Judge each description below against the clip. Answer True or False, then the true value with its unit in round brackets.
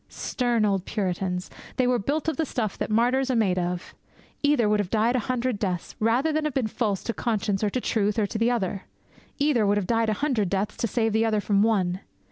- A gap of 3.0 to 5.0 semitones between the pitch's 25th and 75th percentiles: True (3.7 semitones)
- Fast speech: True (235 wpm)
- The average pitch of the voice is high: True (220 Hz)